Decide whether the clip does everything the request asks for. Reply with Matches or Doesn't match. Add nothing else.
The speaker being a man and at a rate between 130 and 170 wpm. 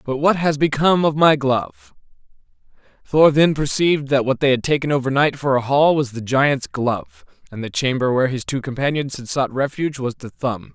Doesn't match